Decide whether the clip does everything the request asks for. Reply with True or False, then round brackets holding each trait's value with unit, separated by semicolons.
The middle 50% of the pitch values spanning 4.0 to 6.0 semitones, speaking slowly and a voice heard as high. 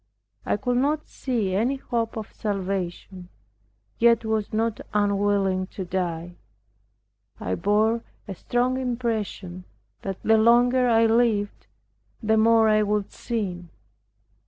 False (3.2 semitones; 120 wpm; 215 Hz)